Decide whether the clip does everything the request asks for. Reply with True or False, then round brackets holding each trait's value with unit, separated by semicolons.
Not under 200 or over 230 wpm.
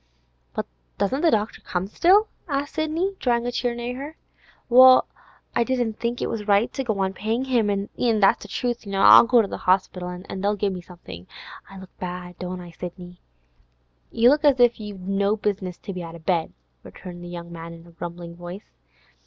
True (205 wpm)